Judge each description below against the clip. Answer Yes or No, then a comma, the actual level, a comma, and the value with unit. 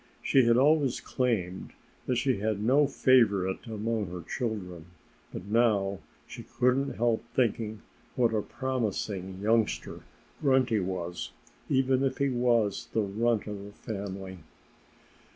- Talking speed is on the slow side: Yes, slow, 130 wpm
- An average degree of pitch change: Yes, average, 4.3 semitones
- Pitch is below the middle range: Yes, low, 110 Hz